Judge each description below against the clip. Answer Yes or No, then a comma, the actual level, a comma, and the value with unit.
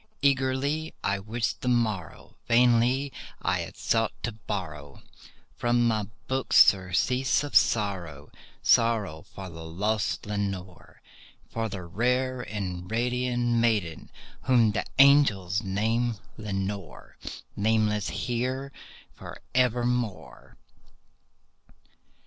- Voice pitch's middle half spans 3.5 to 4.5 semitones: Yes, average, 4.1 semitones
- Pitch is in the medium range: No, low, 110 Hz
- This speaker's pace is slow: Yes, slow, 95 wpm